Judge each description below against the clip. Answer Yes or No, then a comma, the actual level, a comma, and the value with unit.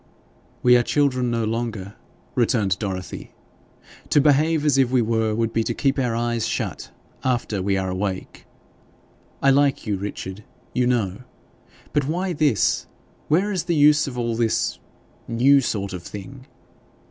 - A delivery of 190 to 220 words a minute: No, average, 155 wpm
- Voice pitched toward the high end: No, low, 120 Hz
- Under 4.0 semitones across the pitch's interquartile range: No, average, 4.7 semitones